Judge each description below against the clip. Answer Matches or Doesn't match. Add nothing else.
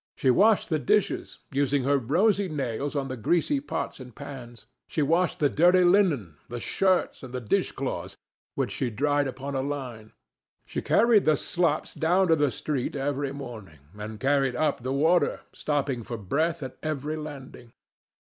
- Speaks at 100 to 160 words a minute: Doesn't match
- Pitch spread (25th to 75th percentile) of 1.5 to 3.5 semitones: Doesn't match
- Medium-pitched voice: Matches